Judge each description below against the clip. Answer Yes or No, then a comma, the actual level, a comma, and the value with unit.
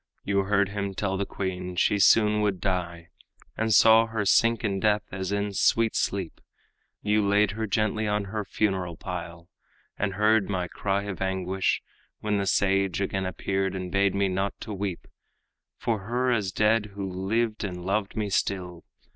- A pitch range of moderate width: No, narrow, 1.9 semitones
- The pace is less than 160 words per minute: No, average, 170 wpm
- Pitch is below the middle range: Yes, low, 100 Hz